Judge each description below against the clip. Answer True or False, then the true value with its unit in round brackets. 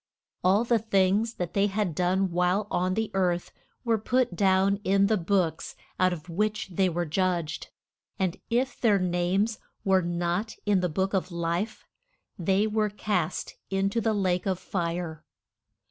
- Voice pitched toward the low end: False (190 Hz)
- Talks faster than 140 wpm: True (160 wpm)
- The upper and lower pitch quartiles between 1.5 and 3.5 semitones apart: True (2.7 semitones)